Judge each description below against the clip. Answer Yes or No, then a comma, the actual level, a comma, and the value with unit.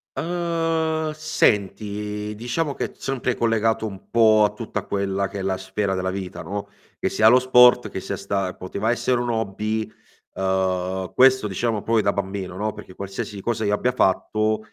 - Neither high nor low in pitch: No, low, 105 Hz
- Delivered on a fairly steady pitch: No, average, 3.5 semitones